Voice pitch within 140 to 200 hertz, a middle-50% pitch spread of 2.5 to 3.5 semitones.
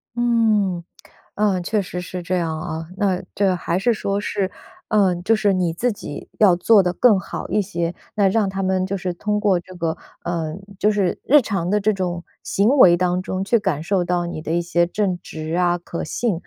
Yes: medium, 185 Hz; average, 2.9 semitones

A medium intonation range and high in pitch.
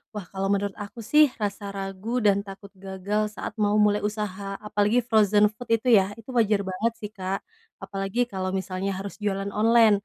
No: narrow, 1.7 semitones; high, 205 Hz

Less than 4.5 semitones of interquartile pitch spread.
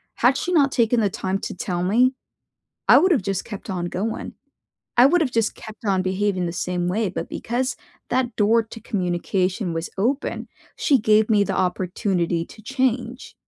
No: average, 4.8 semitones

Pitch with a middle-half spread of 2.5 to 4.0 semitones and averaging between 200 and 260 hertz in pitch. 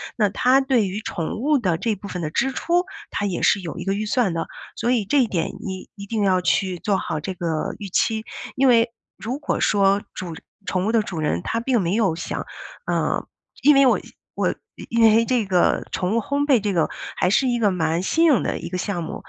No: average, 4.8 semitones; high, 205 Hz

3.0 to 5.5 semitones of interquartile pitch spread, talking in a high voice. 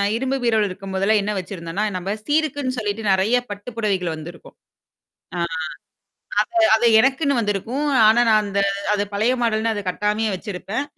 Yes: average, 3.5 semitones; high, 210 Hz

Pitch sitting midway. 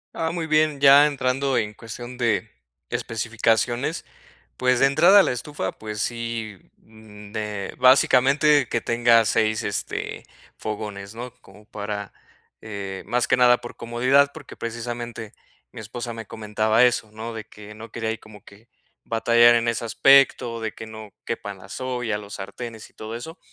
No: low, 115 Hz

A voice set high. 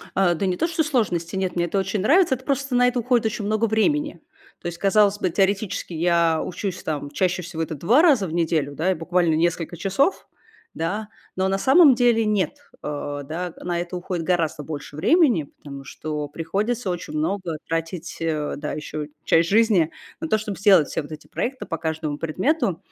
No: medium, 180 Hz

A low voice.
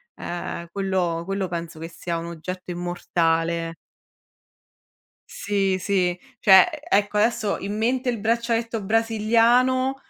No: high, 195 Hz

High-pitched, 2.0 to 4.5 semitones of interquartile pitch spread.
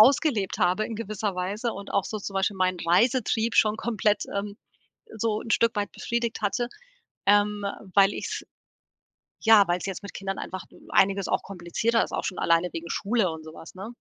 Yes: high, 205 Hz; average, 2.9 semitones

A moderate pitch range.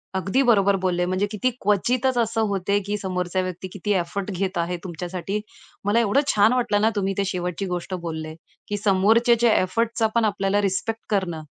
Yes: average, 3.0 semitones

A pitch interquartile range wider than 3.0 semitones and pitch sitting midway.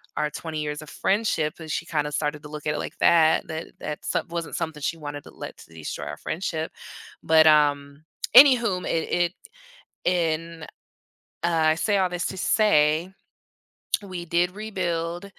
No: average, 2.7 semitones; medium, 160 Hz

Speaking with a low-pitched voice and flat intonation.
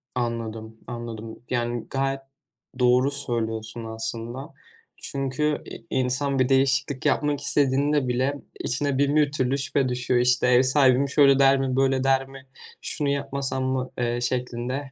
Yes: low, 130 Hz; narrow, 2.2 semitones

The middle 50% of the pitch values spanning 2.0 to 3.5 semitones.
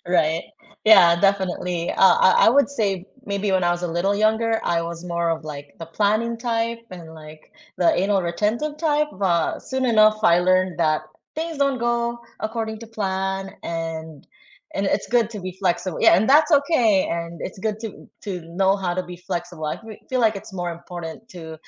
No: average, 4.7 semitones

